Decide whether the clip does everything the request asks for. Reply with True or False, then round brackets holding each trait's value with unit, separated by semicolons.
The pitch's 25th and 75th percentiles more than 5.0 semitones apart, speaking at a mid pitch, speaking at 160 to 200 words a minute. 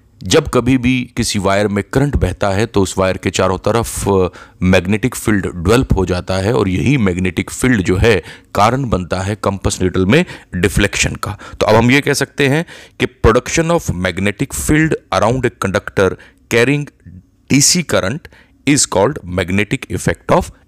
False (5.6 semitones; 100 Hz; 170 wpm)